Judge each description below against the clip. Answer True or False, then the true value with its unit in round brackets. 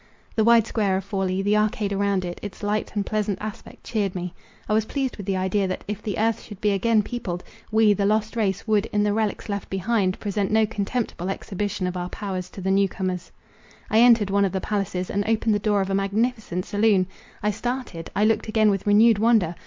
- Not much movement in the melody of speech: True (2.2 semitones)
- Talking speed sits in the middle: False (220 wpm)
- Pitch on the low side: False (205 Hz)